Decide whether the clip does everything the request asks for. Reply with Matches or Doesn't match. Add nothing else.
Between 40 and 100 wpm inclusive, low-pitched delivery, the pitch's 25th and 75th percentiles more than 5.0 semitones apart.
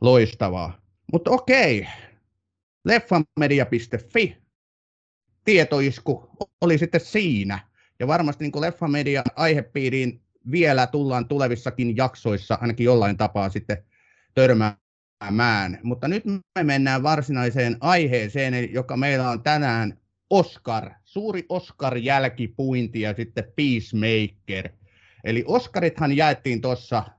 Matches